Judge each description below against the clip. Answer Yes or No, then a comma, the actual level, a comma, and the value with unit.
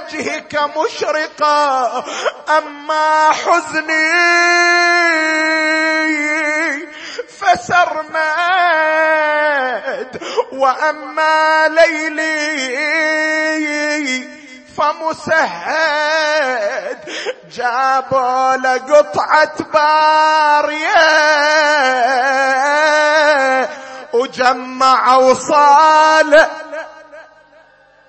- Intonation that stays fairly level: Yes, narrow, 1.1 semitones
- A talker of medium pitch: No, very high, 310 Hz